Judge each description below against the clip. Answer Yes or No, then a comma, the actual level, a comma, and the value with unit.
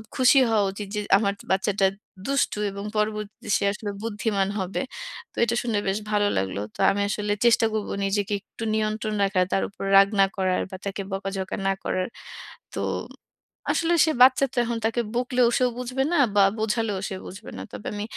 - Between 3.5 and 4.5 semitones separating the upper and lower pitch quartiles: No, average, 2.9 semitones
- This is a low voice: No, high, 210 Hz